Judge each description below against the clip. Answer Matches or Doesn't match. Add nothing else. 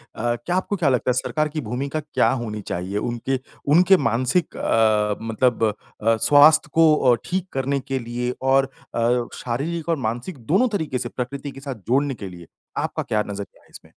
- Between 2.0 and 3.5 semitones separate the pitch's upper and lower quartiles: Doesn't match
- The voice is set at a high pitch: Doesn't match